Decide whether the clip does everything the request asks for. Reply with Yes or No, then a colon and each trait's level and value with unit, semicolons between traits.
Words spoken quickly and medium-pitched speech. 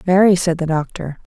No: average, 175 wpm; medium, 170 Hz